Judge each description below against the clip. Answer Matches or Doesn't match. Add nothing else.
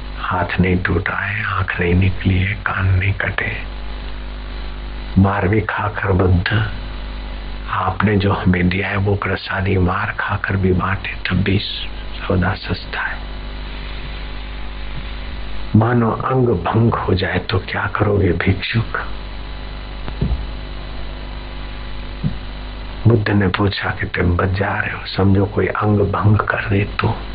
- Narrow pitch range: Matches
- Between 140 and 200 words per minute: Doesn't match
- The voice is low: Matches